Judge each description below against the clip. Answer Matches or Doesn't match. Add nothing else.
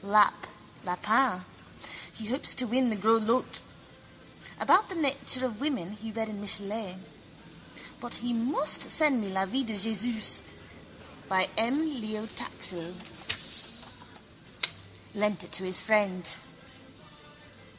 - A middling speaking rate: Doesn't match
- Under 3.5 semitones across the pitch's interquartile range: Doesn't match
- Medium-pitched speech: Doesn't match